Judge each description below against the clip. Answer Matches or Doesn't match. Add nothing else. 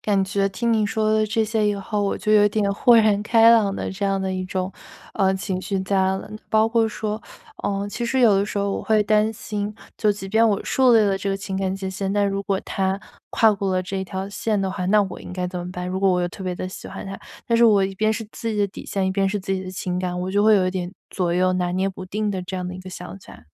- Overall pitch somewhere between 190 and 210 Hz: Matches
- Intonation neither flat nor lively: Doesn't match